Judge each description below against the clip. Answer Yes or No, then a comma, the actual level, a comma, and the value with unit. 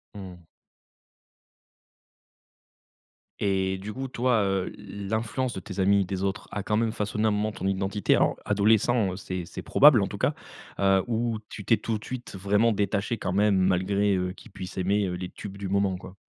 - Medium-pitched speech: No, low, 100 Hz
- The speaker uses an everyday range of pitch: No, narrow, 2.1 semitones